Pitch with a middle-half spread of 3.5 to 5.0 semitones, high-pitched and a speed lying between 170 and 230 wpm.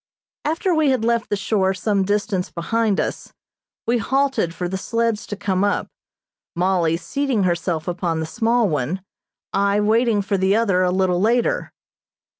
No: average, 4.0 semitones; high, 200 Hz; average, 160 wpm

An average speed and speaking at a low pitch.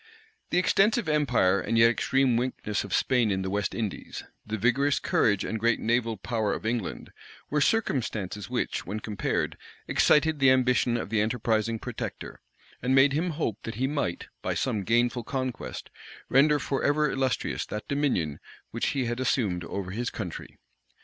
Yes: average, 165 wpm; low, 120 Hz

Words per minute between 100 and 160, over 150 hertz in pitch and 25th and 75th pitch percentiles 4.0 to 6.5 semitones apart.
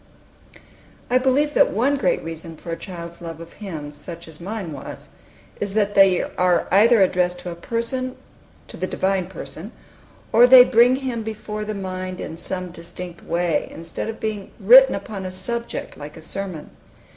No: average, 175 wpm; high, 190 Hz; average, 4.7 semitones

